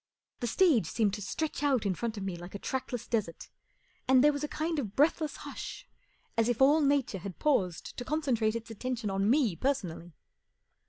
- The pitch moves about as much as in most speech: No, wide, 6.1 semitones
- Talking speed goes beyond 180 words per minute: Yes, average, 195 wpm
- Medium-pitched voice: No, high, 235 Hz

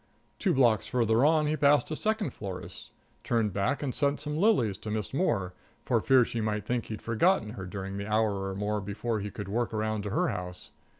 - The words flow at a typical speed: No, fast, 215 wpm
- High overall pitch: No, low, 110 Hz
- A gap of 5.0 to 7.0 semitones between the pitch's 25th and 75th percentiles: Yes, average, 5.3 semitones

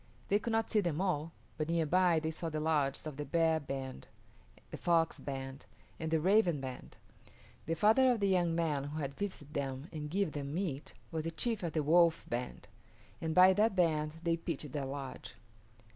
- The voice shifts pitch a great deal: No, average, 3.4 semitones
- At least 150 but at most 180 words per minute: No, average, 200 wpm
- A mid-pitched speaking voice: Yes, medium, 160 Hz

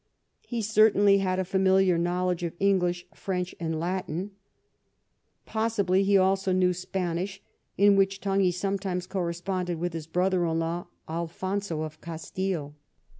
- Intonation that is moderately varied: No, narrow, 2.1 semitones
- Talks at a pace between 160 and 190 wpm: No, slow, 135 wpm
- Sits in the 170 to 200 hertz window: Yes, medium, 185 Hz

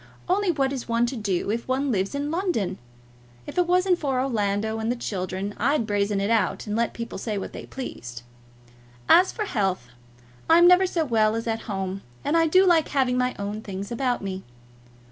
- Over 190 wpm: Yes, average, 200 wpm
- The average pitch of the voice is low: No, high, 235 Hz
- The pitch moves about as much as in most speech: No, wide, 6.3 semitones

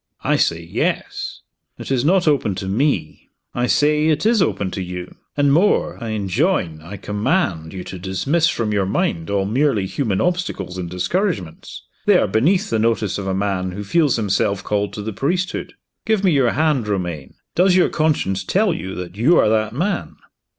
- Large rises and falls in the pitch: Yes, wide, 8.5 semitones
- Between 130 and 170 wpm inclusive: No, average, 185 wpm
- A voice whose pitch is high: No, low, 110 Hz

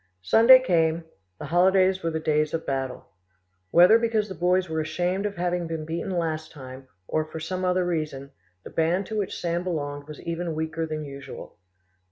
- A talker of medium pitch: Yes, medium, 165 Hz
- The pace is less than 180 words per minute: No, average, 185 wpm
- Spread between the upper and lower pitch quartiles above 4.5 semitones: No, average, 2.9 semitones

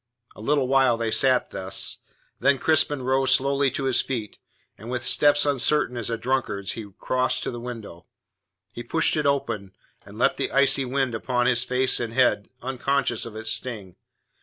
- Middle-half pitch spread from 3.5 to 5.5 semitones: No, average, 2.7 semitones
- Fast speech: No, average, 180 wpm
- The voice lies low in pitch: Yes, low, 125 Hz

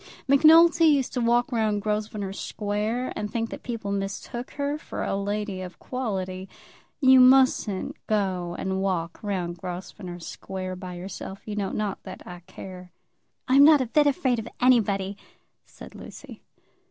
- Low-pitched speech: No, high, 210 Hz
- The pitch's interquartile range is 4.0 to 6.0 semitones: Yes, average, 4.9 semitones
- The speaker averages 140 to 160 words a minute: Yes, average, 155 wpm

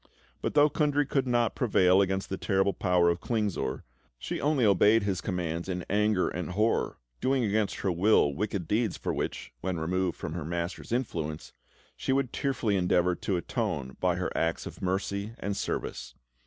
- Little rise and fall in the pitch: No, average, 3.9 semitones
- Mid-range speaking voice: No, very low, 95 Hz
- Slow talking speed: No, average, 175 wpm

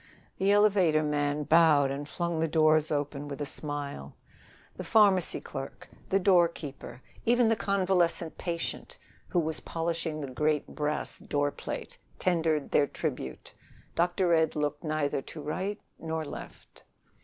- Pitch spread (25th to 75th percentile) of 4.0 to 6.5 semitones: No, average, 3.1 semitones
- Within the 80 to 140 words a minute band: Yes, slow, 135 wpm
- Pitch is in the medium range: Yes, medium, 155 Hz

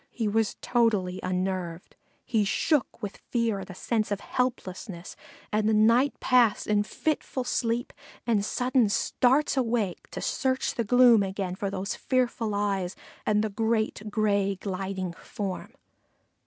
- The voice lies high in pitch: Yes, high, 215 Hz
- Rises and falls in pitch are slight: No, average, 3.5 semitones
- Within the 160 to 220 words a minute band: No, average, 140 wpm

